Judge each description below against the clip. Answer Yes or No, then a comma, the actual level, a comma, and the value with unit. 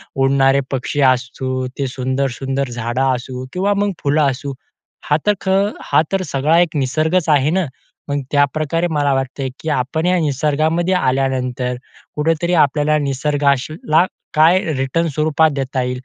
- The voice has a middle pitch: Yes, medium, 145 Hz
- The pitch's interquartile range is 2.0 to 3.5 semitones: Yes, average, 3.1 semitones